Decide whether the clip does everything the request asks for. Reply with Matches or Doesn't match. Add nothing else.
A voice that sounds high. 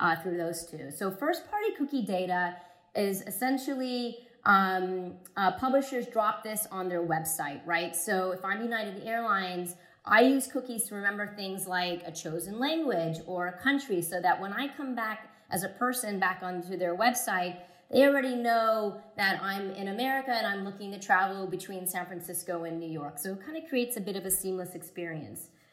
Matches